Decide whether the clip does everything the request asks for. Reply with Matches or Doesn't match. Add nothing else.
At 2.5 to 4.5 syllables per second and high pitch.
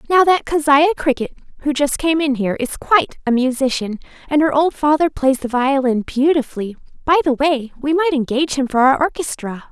Doesn't match